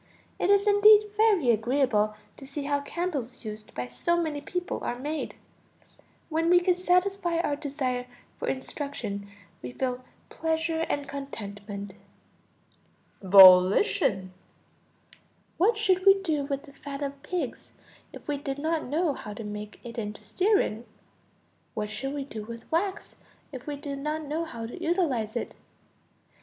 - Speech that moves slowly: No, average, 150 wpm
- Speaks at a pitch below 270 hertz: No, very high, 280 Hz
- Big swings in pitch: Yes, wide, 6.8 semitones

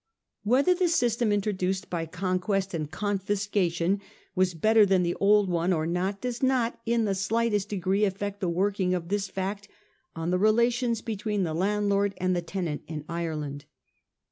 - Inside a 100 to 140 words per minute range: No, average, 165 wpm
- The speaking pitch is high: Yes, high, 195 Hz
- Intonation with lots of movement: No, average, 2.8 semitones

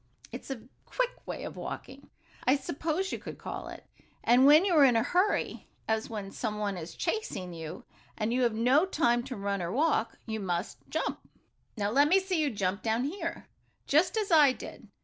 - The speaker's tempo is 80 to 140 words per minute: No, fast, 205 wpm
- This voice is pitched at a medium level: No, very high, 250 Hz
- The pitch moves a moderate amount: No, wide, 7.3 semitones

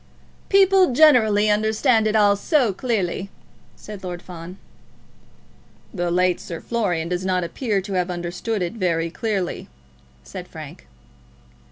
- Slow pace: Yes, slow, 130 wpm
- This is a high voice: Yes, high, 200 Hz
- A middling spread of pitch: Yes, average, 3.9 semitones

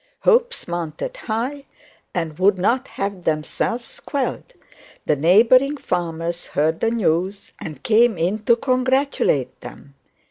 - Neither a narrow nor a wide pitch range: No, wide, 7.4 semitones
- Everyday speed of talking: No, slow, 120 wpm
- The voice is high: Yes, high, 205 Hz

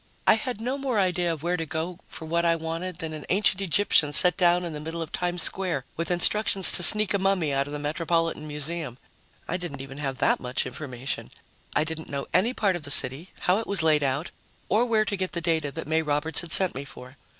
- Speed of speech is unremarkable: No, fast, 240 wpm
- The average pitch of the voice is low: No, medium, 165 Hz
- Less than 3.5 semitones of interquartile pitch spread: No, average, 3.8 semitones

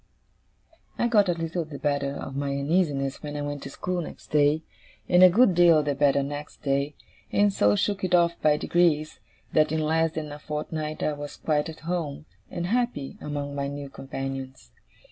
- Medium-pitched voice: Yes, medium, 150 Hz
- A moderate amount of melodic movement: Yes, average, 3.1 semitones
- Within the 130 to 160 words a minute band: No, average, 190 wpm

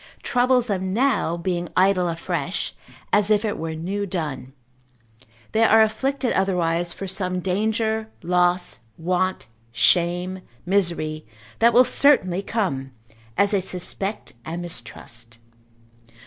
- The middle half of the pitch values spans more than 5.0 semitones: No, average, 3.5 semitones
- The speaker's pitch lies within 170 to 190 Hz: Yes, medium, 185 Hz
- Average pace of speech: No, slow, 120 wpm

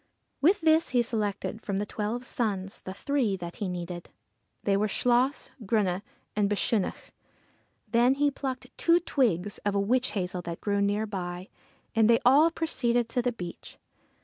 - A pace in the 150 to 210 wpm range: Yes, average, 165 wpm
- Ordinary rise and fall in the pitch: Yes, average, 4.3 semitones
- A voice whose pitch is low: No, high, 215 Hz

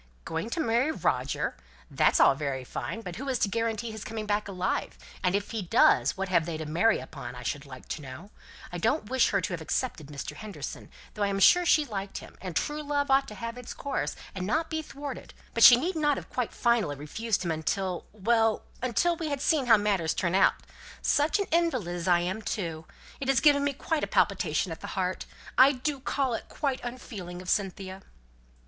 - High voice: Yes, high, 215 Hz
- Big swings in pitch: Yes, wide, 7.1 semitones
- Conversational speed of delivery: No, fast, 220 wpm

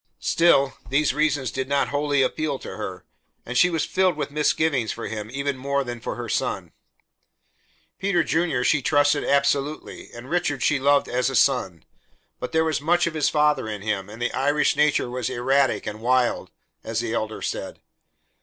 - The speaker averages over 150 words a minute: Yes, average, 180 wpm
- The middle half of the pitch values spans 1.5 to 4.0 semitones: Yes, average, 3.4 semitones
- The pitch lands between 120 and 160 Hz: Yes, medium, 140 Hz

